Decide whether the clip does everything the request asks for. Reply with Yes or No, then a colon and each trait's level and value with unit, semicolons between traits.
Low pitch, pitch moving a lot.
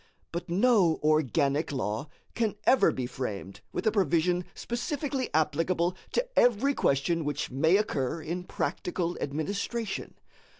No: medium, 170 Hz; wide, 6.4 semitones